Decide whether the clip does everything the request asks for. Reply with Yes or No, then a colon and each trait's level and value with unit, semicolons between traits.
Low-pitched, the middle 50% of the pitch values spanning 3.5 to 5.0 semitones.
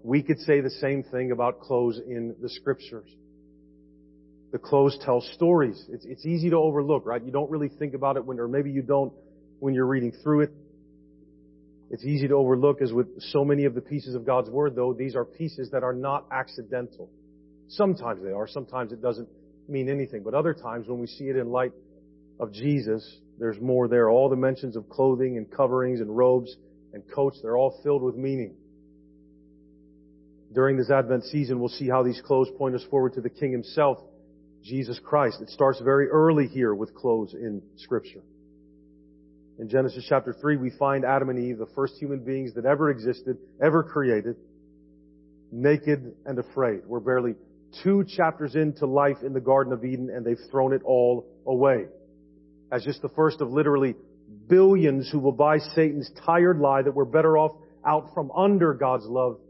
Yes: low, 130 Hz; average, 4.3 semitones